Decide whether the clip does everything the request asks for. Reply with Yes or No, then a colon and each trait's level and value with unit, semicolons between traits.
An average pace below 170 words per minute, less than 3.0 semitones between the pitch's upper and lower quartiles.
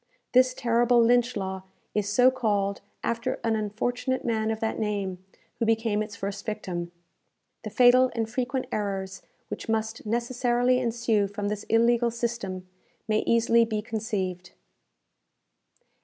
Yes: slow, 135 wpm; narrow, 2.6 semitones